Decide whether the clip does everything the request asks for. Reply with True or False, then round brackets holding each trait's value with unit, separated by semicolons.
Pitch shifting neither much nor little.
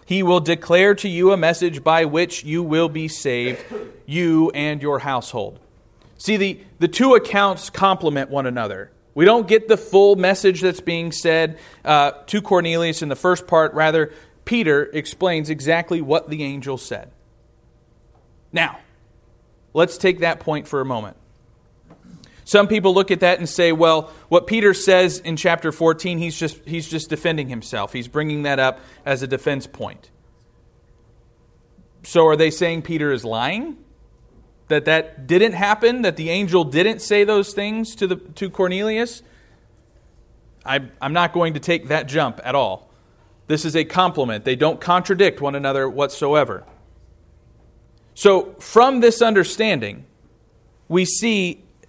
True (4.1 semitones)